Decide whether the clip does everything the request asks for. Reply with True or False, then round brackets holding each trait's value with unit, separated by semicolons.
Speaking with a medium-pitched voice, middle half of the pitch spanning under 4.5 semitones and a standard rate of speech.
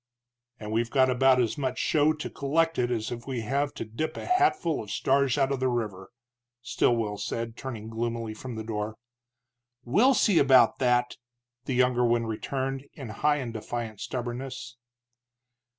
False (125 Hz; 3.1 semitones; 165 wpm)